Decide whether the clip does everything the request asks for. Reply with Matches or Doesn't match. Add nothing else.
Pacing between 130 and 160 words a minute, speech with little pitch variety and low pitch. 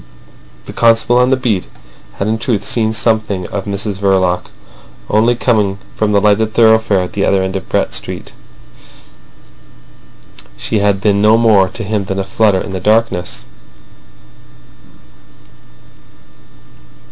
Matches